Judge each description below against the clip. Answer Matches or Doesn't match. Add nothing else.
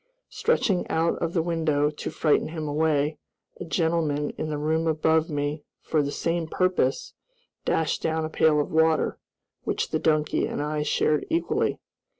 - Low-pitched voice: Doesn't match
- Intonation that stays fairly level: Matches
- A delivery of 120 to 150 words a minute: Doesn't match